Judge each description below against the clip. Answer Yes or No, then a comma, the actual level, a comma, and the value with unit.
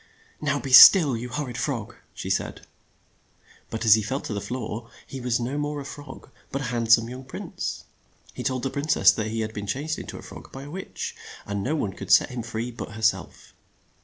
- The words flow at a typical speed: No, fast, 235 wpm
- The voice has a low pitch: Yes, low, 125 Hz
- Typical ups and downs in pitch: Yes, average, 3.8 semitones